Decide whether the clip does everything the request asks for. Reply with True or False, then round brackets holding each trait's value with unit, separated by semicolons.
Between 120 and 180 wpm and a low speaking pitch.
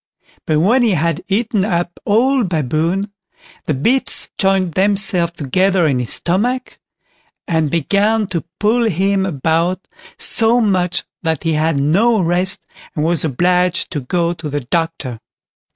False (140 wpm; 180 Hz)